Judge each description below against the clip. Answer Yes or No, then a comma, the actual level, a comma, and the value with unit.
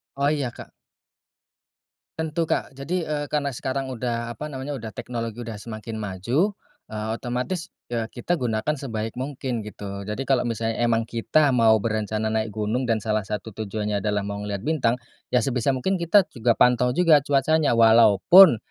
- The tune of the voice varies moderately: Yes, average, 4.1 semitones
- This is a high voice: No, low, 120 Hz